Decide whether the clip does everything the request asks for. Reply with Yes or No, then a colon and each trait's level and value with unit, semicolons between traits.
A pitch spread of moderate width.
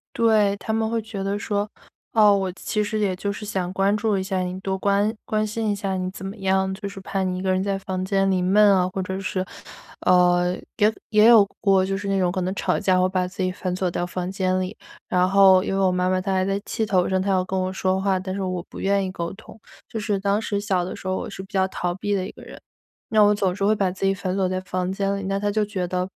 No: narrow, 1.6 semitones